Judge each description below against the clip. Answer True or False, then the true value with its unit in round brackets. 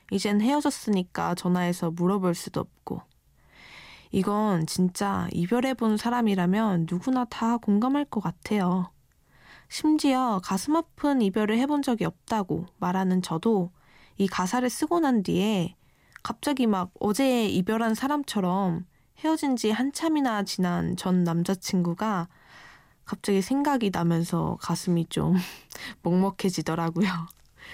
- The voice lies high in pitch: True (200 Hz)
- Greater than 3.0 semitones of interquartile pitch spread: True (5.1 semitones)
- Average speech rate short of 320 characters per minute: True (270 characters per minute)